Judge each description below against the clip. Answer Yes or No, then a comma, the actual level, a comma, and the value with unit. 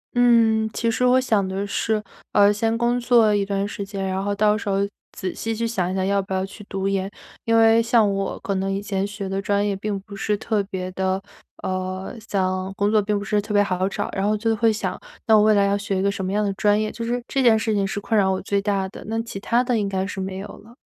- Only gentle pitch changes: Yes, narrow, 2.2 semitones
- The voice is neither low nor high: No, high, 205 Hz